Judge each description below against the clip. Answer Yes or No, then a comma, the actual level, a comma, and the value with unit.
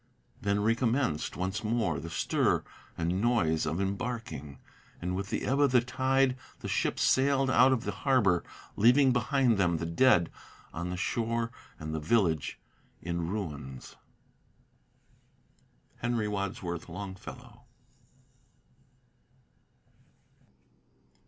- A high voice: No, low, 100 Hz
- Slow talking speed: Yes, slow, 115 wpm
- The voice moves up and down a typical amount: No, wide, 6.2 semitones